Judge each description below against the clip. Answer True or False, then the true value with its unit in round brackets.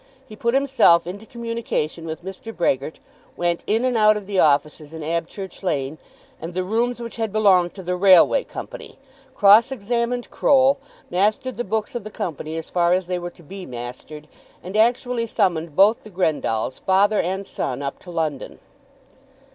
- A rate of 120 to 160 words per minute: False (175 wpm)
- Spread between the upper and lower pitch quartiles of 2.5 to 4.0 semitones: False (5.2 semitones)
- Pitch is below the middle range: False (190 Hz)